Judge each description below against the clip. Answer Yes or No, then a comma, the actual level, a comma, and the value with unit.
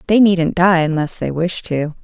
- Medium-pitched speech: Yes, medium, 170 Hz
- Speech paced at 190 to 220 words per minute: Yes, fast, 205 wpm